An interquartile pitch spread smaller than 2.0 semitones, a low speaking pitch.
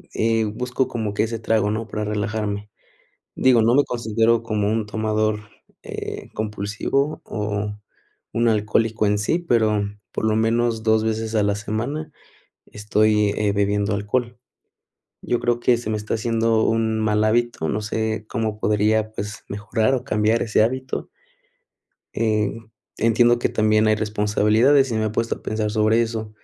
Yes: narrow, 1.5 semitones; low, 110 Hz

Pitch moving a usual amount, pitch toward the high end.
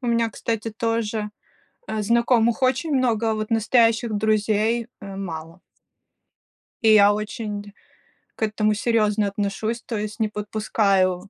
No: narrow, 1.8 semitones; high, 215 Hz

